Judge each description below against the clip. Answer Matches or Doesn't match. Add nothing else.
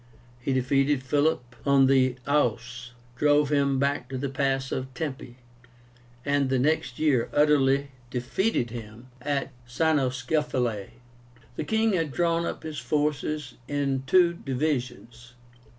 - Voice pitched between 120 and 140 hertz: Matches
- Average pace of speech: Doesn't match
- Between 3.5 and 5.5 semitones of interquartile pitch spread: Doesn't match